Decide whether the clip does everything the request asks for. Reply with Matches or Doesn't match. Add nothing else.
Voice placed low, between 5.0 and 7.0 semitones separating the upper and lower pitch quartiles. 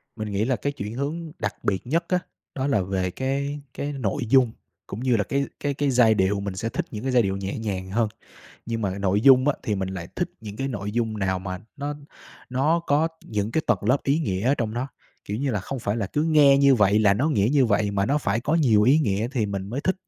Matches